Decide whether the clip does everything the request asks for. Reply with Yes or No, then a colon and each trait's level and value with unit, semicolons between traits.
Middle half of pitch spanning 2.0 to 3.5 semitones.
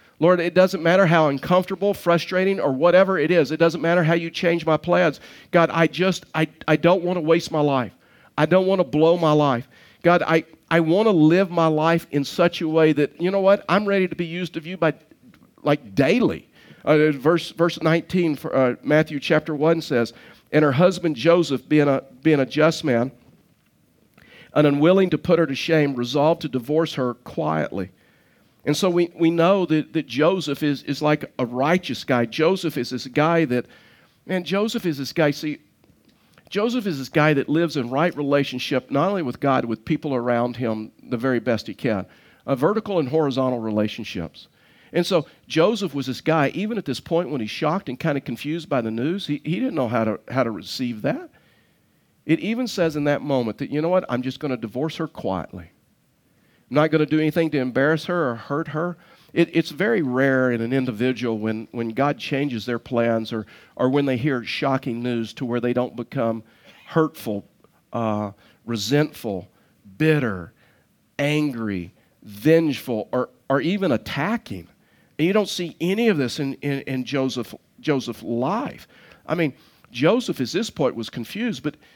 No: average, 4.7 semitones